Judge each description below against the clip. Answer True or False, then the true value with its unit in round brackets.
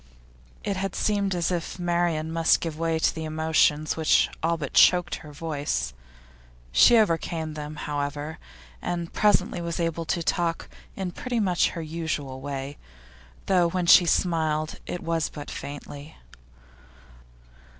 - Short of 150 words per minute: True (140 wpm)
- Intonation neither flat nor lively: False (2.3 semitones)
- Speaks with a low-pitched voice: False (165 Hz)